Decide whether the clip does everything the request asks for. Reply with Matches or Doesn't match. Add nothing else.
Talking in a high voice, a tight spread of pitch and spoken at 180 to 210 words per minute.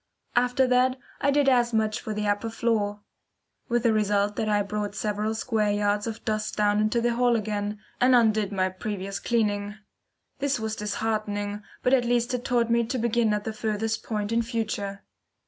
Matches